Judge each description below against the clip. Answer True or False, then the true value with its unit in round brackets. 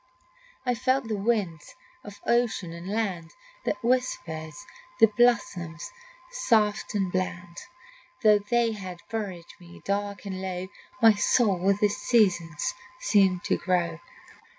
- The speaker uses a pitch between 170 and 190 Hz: False (200 Hz)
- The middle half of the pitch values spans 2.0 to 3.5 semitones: False (4.1 semitones)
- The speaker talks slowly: True (130 wpm)